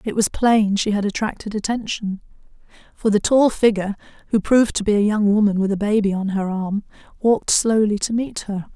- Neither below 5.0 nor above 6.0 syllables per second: Yes, 5.6 syllables/s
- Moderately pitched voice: No, high, 210 Hz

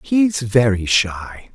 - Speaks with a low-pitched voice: Yes, low, 130 Hz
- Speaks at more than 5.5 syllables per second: No, 2.8 syllables/s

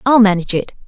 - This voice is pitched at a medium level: No, high, 210 Hz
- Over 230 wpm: No, fast, 205 wpm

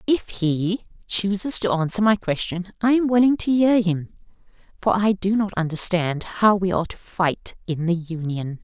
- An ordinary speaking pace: Yes, average, 180 wpm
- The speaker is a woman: Yes, female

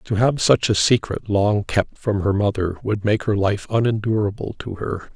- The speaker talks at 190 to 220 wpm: Yes, average, 200 wpm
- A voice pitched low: Yes, low, 105 Hz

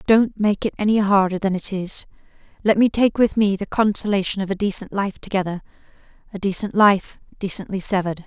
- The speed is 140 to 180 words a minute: Yes, average, 175 wpm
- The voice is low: No, high, 200 Hz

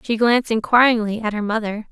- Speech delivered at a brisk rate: No, average, 190 wpm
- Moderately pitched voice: No, high, 225 Hz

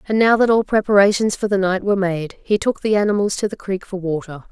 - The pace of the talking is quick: Yes, fast, 250 wpm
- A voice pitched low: No, high, 200 Hz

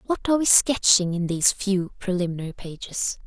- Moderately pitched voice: No, high, 195 Hz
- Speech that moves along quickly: No, average, 165 wpm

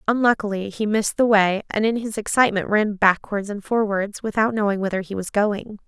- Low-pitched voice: No, high, 210 Hz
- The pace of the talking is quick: No, average, 195 wpm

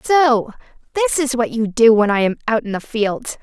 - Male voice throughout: No, female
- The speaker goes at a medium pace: No, fast, 230 wpm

